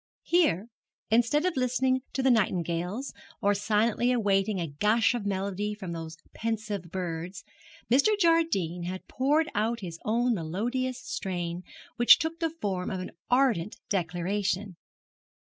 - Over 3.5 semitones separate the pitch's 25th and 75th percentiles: Yes, wide, 5.6 semitones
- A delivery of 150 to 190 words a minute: No, slow, 135 wpm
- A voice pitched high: Yes, high, 210 Hz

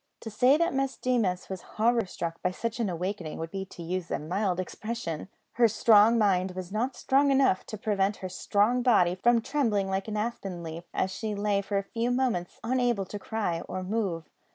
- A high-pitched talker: Yes, high, 205 Hz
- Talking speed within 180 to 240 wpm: Yes, average, 200 wpm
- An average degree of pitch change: Yes, average, 4.1 semitones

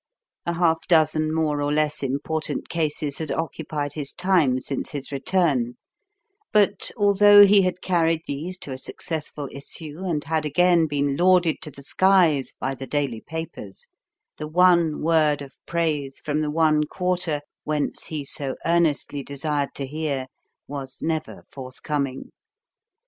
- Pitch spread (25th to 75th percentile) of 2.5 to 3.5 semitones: Yes, average, 2.9 semitones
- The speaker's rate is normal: Yes, average, 145 wpm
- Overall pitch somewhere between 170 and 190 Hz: No, medium, 155 Hz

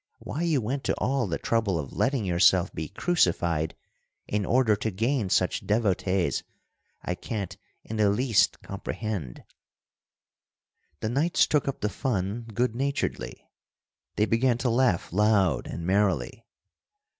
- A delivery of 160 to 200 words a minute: No, slow, 135 wpm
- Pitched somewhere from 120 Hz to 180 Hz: No, low, 105 Hz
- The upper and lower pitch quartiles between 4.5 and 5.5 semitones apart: Yes, average, 4.9 semitones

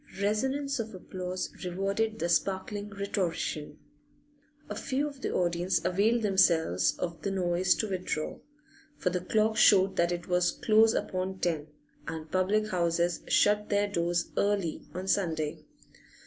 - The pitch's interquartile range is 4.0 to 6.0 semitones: No, average, 3.2 semitones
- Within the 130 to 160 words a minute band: Yes, average, 140 wpm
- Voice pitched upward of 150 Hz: Yes, medium, 185 Hz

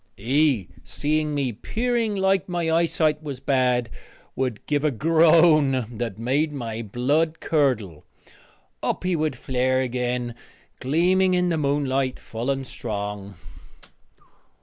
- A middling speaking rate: No, slow, 125 wpm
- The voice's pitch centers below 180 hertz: Yes, medium, 140 Hz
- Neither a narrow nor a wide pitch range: Yes, average, 4.6 semitones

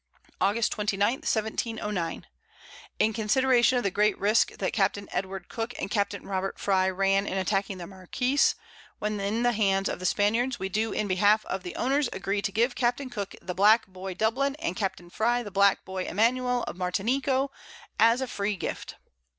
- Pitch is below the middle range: No, high, 210 Hz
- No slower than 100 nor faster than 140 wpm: No, average, 180 wpm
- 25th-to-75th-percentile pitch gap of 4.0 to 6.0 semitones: No, average, 3.6 semitones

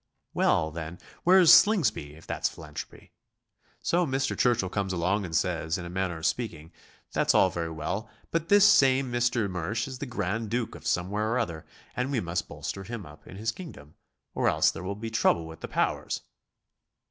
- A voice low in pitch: Yes, low, 100 Hz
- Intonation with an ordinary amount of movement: No, wide, 6.4 semitones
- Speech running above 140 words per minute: Yes, average, 190 wpm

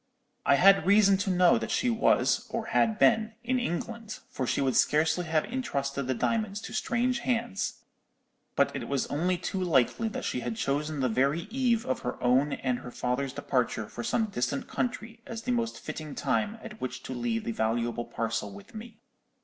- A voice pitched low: No, medium, 170 Hz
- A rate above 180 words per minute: Yes, average, 190 wpm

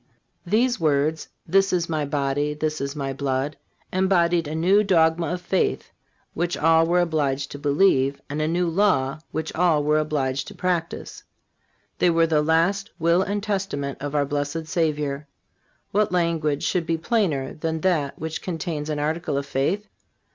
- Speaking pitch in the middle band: Yes, medium, 160 Hz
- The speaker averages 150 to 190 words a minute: Yes, average, 165 wpm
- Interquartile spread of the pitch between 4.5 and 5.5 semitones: No, average, 3.3 semitones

